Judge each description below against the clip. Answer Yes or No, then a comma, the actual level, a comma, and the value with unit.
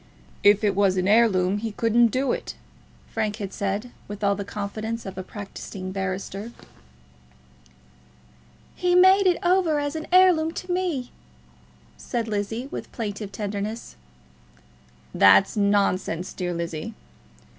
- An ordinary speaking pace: No, slow, 130 wpm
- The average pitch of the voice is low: No, high, 210 Hz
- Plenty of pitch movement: No, average, 4.0 semitones